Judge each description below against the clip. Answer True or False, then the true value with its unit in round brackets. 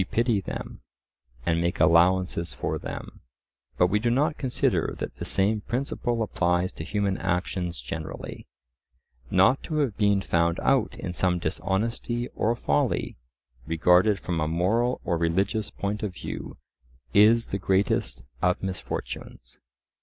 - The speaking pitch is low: True (95 Hz)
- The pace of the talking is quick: False (140 wpm)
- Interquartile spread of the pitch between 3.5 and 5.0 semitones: True (4.2 semitones)